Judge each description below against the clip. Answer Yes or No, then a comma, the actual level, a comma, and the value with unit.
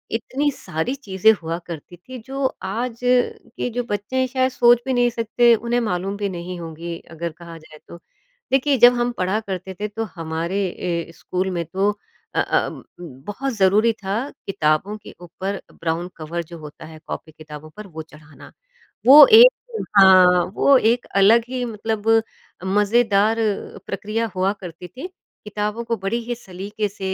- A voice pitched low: No, high, 200 Hz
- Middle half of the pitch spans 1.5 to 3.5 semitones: No, wide, 5.4 semitones